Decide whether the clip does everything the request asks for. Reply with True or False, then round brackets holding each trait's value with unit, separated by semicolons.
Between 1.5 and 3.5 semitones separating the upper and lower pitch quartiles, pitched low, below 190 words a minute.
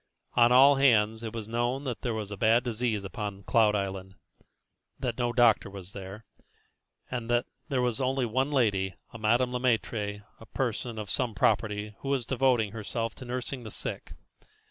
True (3.0 semitones; 115 Hz; 170 wpm)